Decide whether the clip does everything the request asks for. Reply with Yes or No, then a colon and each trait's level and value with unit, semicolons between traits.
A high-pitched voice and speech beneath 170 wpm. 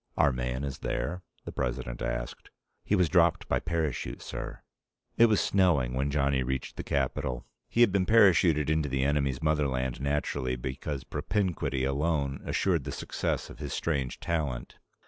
No: very low, 70 Hz; average, 160 wpm